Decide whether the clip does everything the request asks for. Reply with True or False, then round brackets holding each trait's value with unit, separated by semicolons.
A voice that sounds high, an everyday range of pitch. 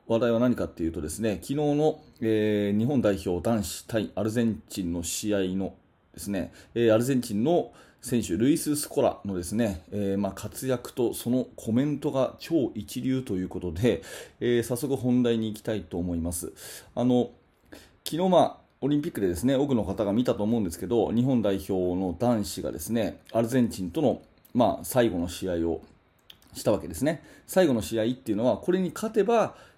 False (110 Hz; 4.9 semitones)